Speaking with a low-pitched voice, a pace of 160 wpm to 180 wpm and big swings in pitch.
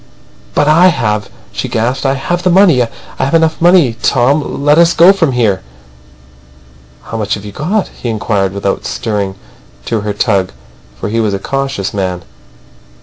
Yes: low, 120 Hz; average, 170 wpm; wide, 7.4 semitones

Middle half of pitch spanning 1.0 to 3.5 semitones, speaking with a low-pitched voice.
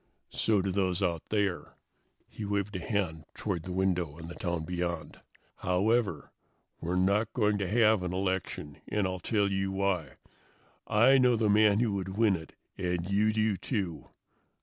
Yes: average, 2.9 semitones; very low, 95 Hz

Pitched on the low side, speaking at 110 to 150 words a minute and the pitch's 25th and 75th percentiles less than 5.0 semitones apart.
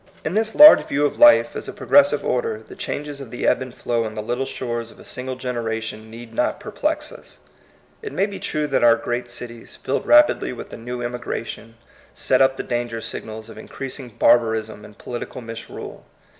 No: low, 120 Hz; average, 200 wpm; average, 4.2 semitones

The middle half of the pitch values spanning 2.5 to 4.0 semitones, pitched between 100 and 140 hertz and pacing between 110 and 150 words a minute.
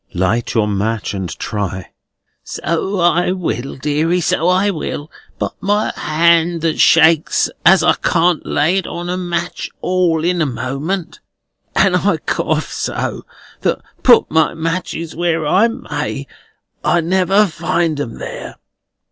No: average, 3.6 semitones; medium, 165 Hz; average, 140 wpm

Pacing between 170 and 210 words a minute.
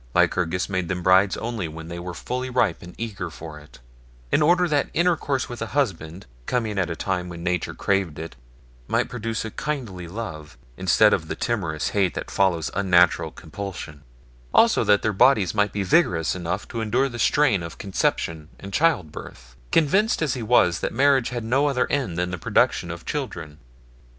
Yes: average, 190 wpm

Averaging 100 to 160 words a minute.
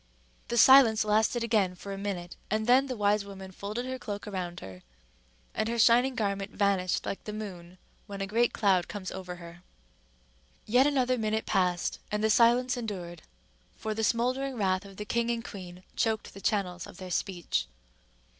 No: average, 180 wpm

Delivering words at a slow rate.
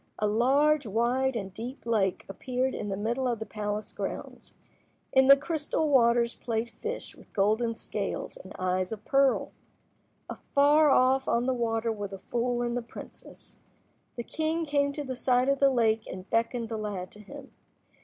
No: average, 175 wpm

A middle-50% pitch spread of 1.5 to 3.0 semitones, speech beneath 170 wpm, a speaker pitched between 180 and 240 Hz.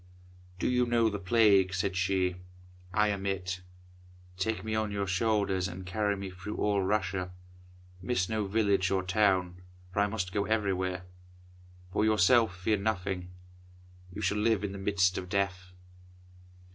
No: narrow, 2.4 semitones; average, 155 wpm; low, 100 Hz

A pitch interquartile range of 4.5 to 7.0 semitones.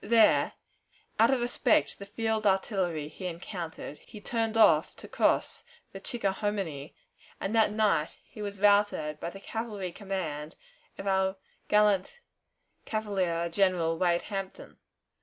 No: average, 3.6 semitones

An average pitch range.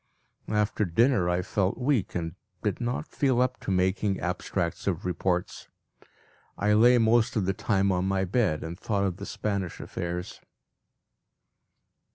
Yes: average, 3.5 semitones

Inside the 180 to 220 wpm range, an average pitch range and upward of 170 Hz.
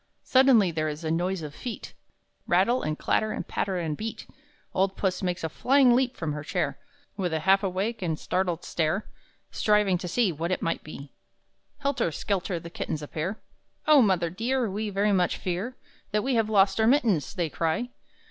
Yes: average, 185 wpm; average, 4.8 semitones; high, 190 Hz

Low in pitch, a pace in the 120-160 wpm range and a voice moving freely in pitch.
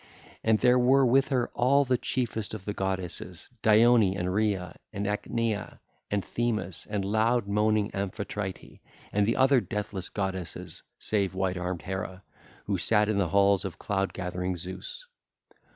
No: low, 100 Hz; average, 150 wpm; average, 3.2 semitones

